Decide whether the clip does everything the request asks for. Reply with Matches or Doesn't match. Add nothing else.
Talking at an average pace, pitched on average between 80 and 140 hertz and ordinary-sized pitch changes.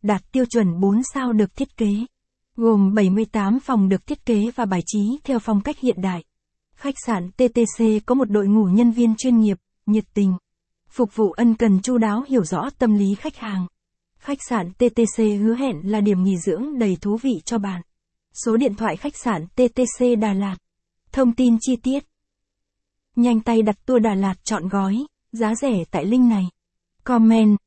Doesn't match